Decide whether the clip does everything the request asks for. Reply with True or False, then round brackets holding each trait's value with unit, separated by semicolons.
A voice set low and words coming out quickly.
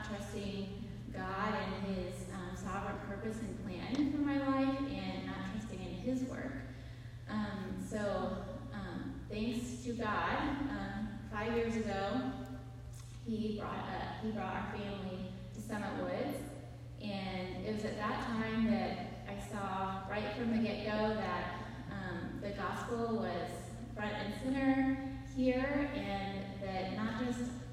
False (125 Hz; 140 wpm)